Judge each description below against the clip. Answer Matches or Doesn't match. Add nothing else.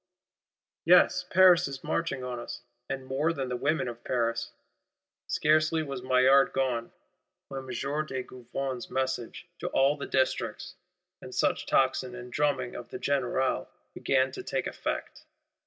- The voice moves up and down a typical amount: Doesn't match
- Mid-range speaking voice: Doesn't match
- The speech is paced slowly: Doesn't match